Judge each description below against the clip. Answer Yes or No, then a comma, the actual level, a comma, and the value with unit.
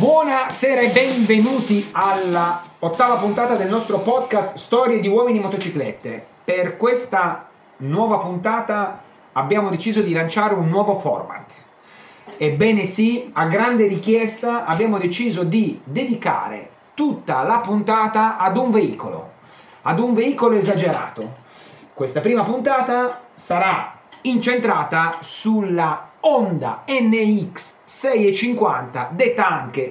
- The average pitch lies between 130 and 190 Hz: No, high, 215 Hz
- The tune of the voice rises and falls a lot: No, average, 4.4 semitones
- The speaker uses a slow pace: Yes, slow, 105 wpm